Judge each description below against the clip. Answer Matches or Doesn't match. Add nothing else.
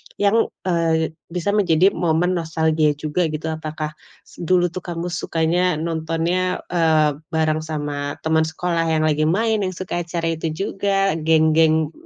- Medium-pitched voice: Matches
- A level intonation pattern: Matches